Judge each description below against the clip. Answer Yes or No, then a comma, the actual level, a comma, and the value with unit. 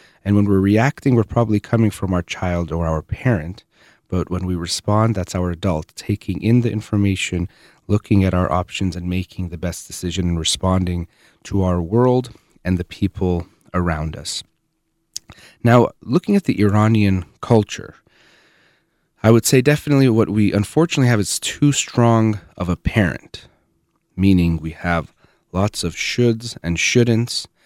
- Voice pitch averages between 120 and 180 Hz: No, low, 100 Hz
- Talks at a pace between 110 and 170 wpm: Yes, average, 155 wpm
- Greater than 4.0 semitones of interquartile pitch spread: Yes, average, 4.4 semitones